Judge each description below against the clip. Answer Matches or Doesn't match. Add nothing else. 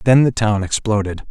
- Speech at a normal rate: Matches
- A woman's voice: Doesn't match